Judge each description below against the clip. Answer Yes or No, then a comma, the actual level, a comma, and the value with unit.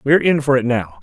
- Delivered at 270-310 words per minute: Yes, fast, 295 wpm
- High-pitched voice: No, low, 130 Hz